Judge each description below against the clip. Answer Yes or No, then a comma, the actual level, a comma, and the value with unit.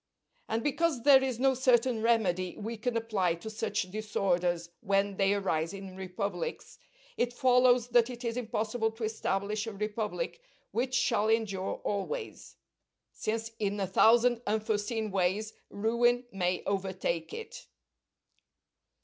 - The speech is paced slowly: Yes, slow, 130 wpm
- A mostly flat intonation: No, average, 3.6 semitones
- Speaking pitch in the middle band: No, high, 215 Hz